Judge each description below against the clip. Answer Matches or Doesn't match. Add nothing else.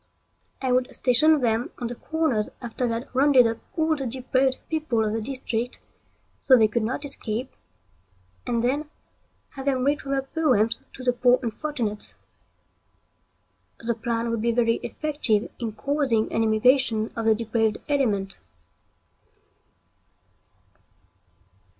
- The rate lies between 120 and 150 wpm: Matches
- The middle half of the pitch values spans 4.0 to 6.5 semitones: Doesn't match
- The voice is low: Doesn't match